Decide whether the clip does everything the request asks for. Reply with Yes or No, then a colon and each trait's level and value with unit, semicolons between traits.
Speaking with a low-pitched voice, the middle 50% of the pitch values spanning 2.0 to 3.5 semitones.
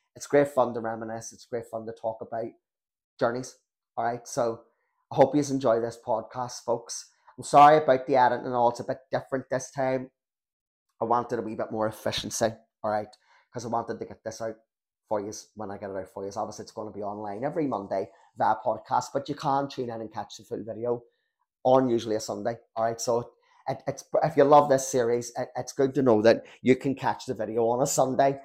Yes: low, 120 Hz; average, 3.0 semitones